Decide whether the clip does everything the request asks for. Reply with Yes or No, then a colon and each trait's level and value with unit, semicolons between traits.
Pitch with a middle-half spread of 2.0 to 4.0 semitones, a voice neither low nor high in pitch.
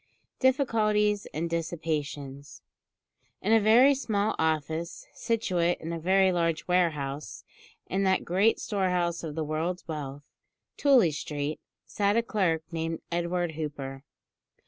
No: average, 4.5 semitones; medium, 170 Hz